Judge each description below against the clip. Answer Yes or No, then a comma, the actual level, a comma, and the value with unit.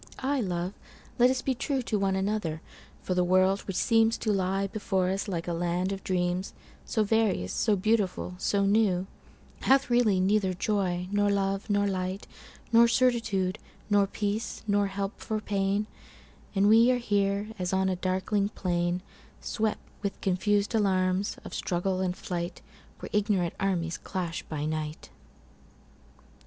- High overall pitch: Yes, high, 195 Hz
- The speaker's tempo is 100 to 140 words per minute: Yes, slow, 135 wpm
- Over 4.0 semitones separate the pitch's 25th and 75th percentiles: No, narrow, 2.4 semitones